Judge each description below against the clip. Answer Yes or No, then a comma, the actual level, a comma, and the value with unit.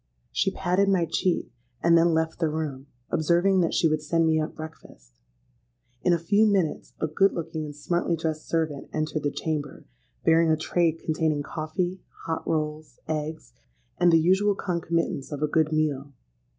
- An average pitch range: No, narrow, 1.9 semitones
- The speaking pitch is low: No, medium, 160 Hz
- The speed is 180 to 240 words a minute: No, average, 170 wpm